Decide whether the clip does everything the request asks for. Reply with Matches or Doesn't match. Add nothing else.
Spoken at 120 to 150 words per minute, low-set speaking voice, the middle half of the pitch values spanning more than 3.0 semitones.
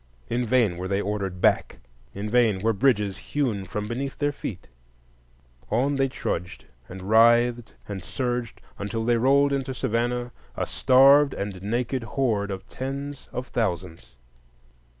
Matches